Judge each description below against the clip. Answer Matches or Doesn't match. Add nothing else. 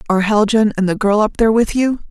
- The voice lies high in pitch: Matches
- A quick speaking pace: Matches